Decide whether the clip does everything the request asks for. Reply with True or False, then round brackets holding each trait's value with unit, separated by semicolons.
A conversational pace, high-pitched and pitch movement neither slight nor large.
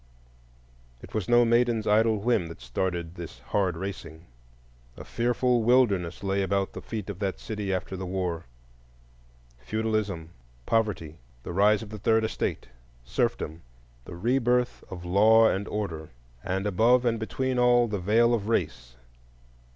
False (145 wpm; 100 Hz; 4.7 semitones)